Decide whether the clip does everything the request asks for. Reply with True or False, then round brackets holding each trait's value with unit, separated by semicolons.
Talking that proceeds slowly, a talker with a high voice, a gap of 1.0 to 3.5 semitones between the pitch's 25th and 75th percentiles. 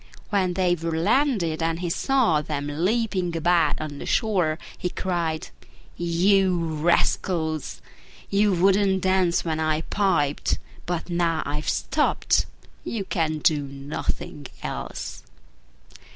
False (120 wpm; 170 Hz; 3.2 semitones)